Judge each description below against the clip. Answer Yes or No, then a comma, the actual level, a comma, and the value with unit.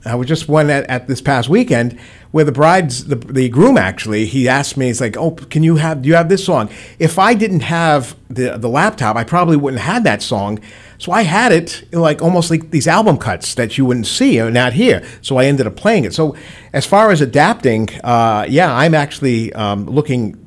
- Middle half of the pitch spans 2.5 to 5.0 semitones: No, wide, 5.4 semitones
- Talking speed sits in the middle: No, fast, 235 wpm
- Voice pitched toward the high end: No, medium, 140 Hz